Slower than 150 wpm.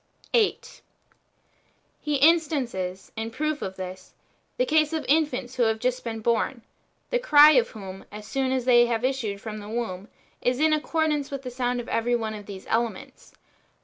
No: average, 180 wpm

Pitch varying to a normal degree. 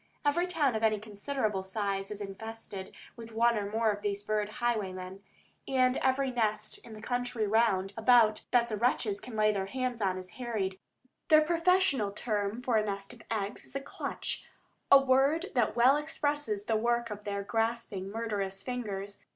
Yes: average, 3.5 semitones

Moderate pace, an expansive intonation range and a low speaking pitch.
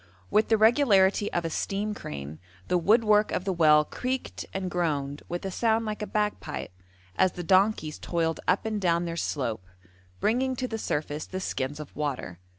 No: average, 180 wpm; wide, 5.8 semitones; medium, 185 Hz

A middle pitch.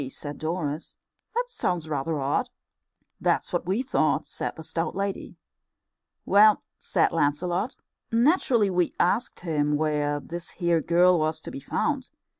Yes: medium, 170 Hz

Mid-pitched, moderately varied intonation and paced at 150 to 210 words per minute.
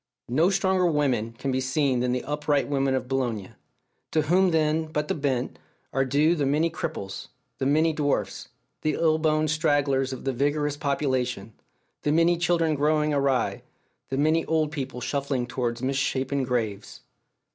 Yes: medium, 145 Hz; average, 3.0 semitones; average, 160 wpm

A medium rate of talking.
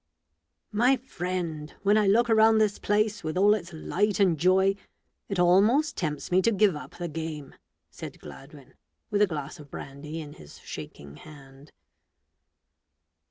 Yes: average, 155 wpm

